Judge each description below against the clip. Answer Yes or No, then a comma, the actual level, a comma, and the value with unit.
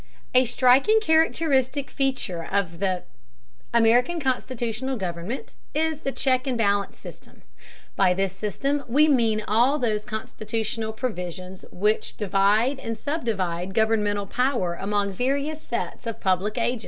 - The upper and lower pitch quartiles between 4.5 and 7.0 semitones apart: Yes, average, 4.8 semitones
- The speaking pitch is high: Yes, high, 225 Hz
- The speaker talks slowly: Yes, slow, 125 wpm